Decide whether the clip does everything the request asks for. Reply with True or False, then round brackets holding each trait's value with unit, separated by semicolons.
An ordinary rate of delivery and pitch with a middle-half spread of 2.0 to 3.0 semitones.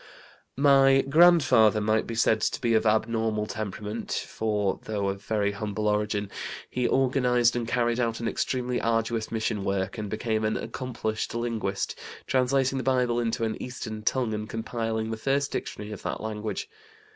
True (160 wpm; 2.5 semitones)